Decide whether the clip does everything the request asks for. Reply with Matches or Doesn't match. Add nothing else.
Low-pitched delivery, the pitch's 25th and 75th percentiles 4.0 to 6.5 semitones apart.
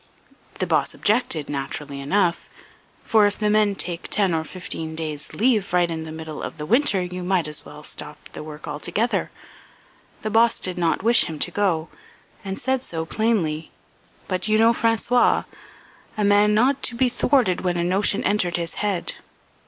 Doesn't match